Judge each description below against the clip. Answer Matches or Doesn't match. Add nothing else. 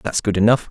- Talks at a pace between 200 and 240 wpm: Doesn't match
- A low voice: Matches